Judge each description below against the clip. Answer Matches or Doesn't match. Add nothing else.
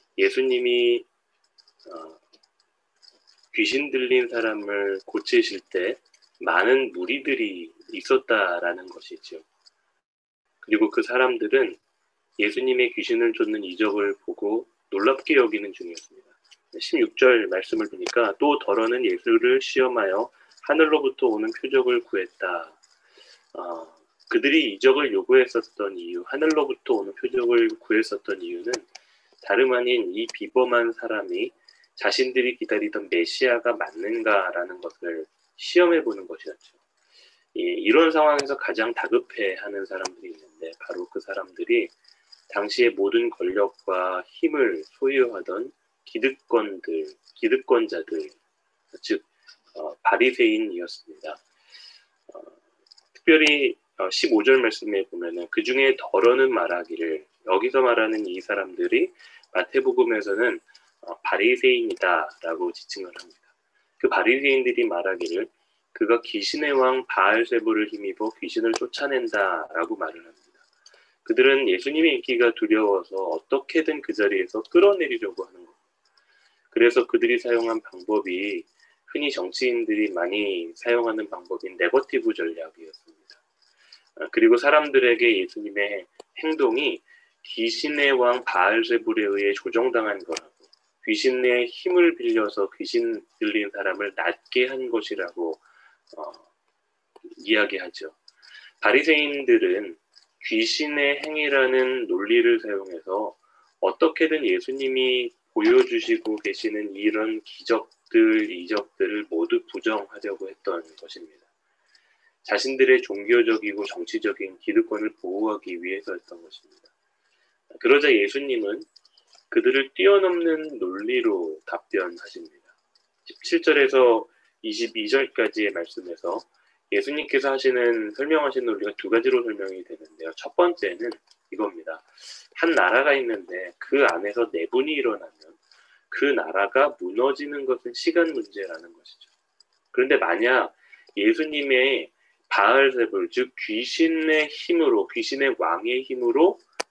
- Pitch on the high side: Matches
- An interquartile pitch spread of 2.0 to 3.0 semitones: Matches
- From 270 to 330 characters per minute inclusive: Matches